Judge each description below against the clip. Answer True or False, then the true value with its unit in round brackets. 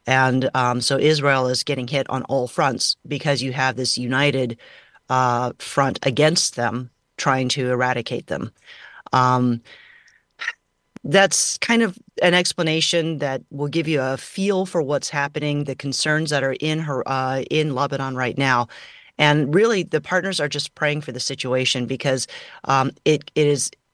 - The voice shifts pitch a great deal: False (3.1 semitones)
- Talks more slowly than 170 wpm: True (160 wpm)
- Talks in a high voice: False (140 Hz)